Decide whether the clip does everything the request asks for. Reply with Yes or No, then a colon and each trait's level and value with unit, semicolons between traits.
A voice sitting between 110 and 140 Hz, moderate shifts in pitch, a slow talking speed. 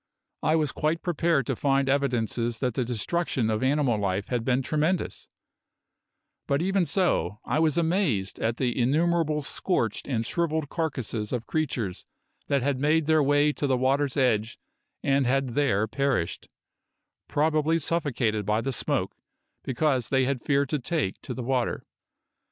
No: low, 135 Hz; average, 4.4 semitones; average, 155 wpm